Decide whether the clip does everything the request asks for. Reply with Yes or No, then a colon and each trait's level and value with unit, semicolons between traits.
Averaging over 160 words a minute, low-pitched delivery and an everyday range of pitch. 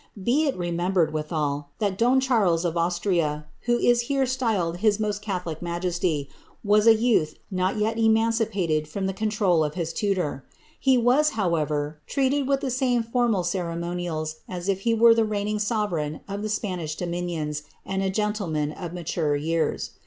No: average, 175 wpm; high, 190 Hz; average, 5.0 semitones